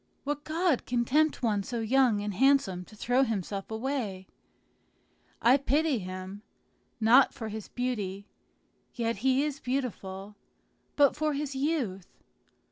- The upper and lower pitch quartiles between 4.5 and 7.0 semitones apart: Yes, average, 5.3 semitones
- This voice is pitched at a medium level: No, high, 245 Hz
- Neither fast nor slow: No, slow, 130 wpm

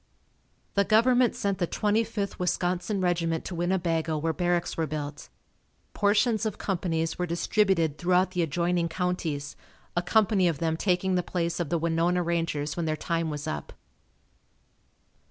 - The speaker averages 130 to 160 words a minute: Yes, average, 155 wpm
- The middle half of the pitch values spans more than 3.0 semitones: No, narrow, 2.5 semitones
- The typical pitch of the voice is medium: Yes, medium, 175 Hz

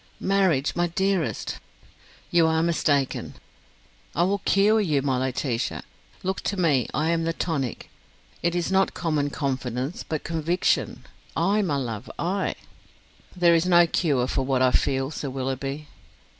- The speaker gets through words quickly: No, average, 150 wpm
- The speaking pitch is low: No, medium, 160 Hz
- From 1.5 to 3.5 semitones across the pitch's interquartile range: No, average, 4.7 semitones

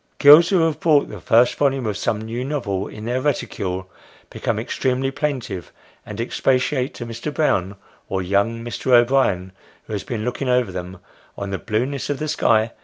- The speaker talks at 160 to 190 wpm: Yes, average, 180 wpm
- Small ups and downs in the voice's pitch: No, average, 4.8 semitones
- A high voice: No, low, 120 Hz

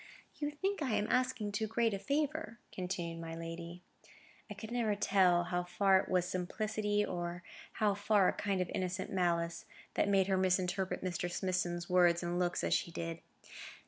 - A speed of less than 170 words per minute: No, average, 175 wpm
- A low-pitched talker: No, medium, 185 Hz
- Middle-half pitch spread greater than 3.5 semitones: No, average, 2.9 semitones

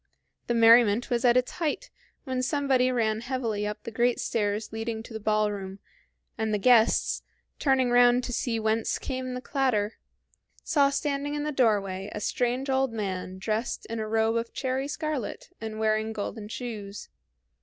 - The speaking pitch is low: No, high, 230 Hz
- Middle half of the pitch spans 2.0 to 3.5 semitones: Yes, average, 3.0 semitones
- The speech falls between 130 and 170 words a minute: Yes, average, 165 wpm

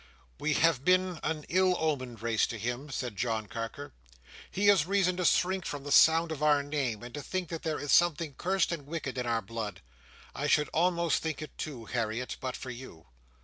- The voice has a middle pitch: Yes, medium, 145 Hz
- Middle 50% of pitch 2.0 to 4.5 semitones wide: No, wide, 5.5 semitones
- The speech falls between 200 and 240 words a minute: Yes, fast, 205 wpm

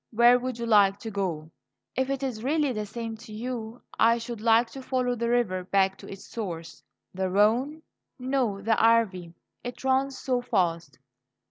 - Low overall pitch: No, high, 230 Hz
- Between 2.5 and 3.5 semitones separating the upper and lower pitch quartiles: No, average, 4.0 semitones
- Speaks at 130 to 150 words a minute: No, average, 175 wpm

